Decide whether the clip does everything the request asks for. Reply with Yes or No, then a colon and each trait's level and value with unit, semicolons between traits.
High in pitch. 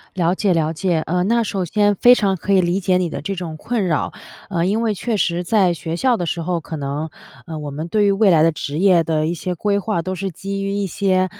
No: medium, 180 Hz